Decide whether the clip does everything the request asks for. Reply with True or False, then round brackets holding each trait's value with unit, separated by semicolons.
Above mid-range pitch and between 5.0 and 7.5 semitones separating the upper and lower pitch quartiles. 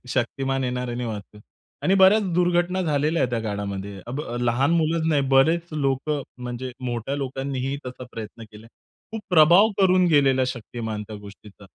False (135 Hz; 5.3 semitones)